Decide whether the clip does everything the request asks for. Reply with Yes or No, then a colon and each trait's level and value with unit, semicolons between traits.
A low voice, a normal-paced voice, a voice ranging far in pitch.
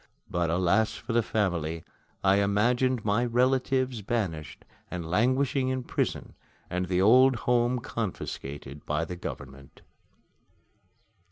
No: low, 105 Hz; slow, 115 wpm; wide, 6.0 semitones